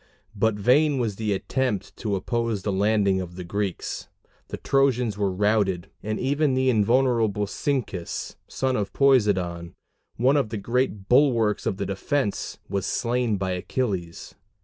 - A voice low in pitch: Yes, low, 105 Hz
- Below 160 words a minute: Yes, average, 150 wpm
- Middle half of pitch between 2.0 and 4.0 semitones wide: No, average, 4.4 semitones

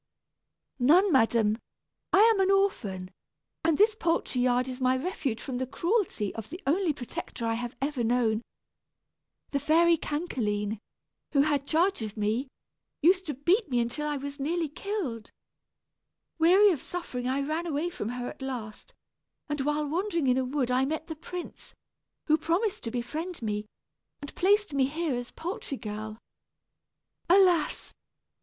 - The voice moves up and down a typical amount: No, wide, 5.9 semitones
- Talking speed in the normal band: Yes, average, 155 wpm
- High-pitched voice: Yes, very high, 285 Hz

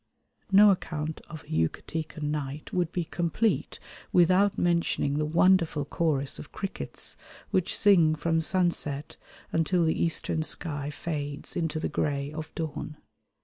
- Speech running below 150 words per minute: Yes, slow, 135 wpm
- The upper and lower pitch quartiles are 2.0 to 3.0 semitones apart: Yes, narrow, 2.6 semitones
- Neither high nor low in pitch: Yes, medium, 160 Hz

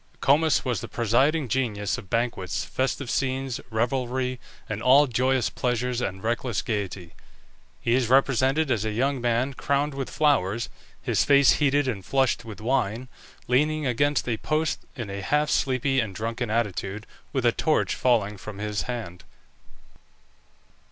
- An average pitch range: Yes, average, 3.6 semitones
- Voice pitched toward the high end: No, low, 125 Hz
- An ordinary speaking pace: Yes, average, 150 wpm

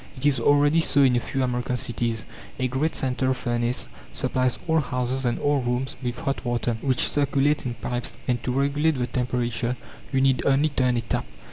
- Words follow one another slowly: No, average, 195 wpm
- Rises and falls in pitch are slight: Yes, narrow, 2.2 semitones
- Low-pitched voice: Yes, low, 130 Hz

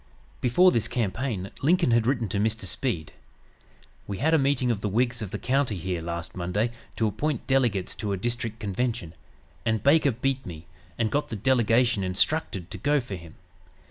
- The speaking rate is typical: Yes, average, 180 wpm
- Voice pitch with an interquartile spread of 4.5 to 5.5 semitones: Yes, average, 5.0 semitones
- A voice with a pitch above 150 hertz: No, low, 115 Hz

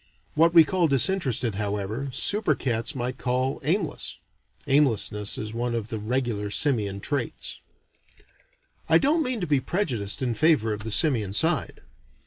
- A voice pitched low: Yes, low, 130 Hz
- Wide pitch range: Yes, wide, 6.4 semitones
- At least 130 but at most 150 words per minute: Yes, average, 145 wpm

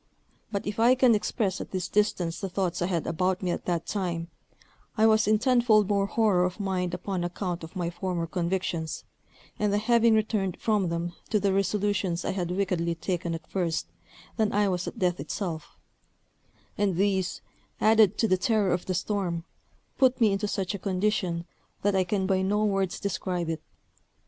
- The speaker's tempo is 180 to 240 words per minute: Yes, average, 185 wpm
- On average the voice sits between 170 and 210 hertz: Yes, high, 190 Hz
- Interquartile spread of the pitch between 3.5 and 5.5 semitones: No, average, 2.9 semitones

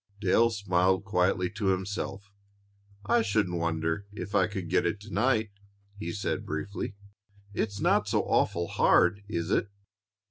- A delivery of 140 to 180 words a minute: Yes, average, 145 wpm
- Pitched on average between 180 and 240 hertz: No, low, 100 Hz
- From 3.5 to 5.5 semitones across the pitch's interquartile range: No, narrow, 2.5 semitones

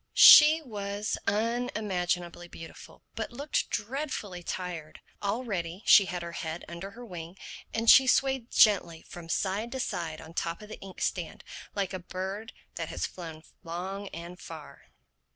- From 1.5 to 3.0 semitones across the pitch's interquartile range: No, average, 4.5 semitones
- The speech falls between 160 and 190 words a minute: No, average, 150 wpm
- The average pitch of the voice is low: No, high, 190 Hz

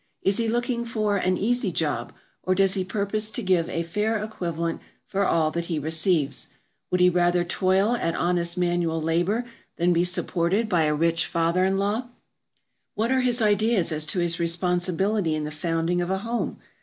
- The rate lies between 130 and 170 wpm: No, average, 185 wpm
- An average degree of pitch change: Yes, average, 3.7 semitones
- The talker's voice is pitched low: No, medium, 180 Hz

